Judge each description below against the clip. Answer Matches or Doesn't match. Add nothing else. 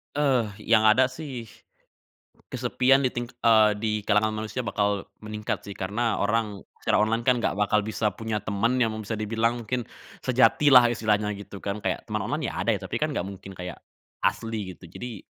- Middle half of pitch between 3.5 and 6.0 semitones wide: Doesn't match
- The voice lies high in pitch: Doesn't match